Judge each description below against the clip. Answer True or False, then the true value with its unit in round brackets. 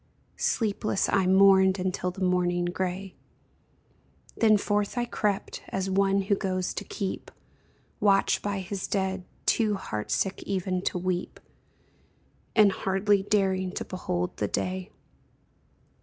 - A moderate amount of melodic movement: False (1.4 semitones)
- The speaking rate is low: True (125 wpm)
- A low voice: False (190 Hz)